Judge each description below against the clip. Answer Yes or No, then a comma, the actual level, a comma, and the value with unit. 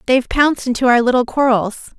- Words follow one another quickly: No, average, 180 wpm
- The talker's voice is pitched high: Yes, very high, 250 Hz